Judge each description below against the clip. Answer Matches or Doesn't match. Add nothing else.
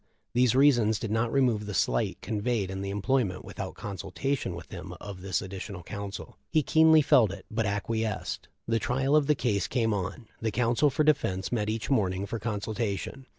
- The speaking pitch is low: Matches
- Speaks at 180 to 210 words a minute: Matches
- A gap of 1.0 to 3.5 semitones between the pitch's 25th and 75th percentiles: Doesn't match